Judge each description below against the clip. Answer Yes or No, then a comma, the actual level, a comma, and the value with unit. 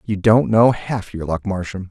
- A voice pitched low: Yes, low, 100 Hz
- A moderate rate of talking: No, fast, 220 wpm